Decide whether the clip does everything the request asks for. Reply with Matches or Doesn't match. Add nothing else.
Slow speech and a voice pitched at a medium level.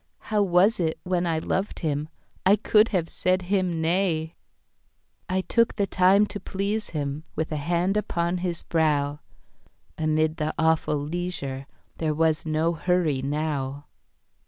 Matches